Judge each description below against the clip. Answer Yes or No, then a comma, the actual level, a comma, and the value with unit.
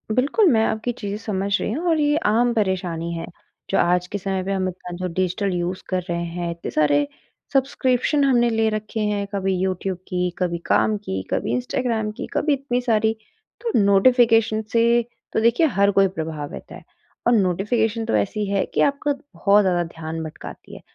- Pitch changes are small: No, average, 4.5 semitones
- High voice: Yes, high, 200 Hz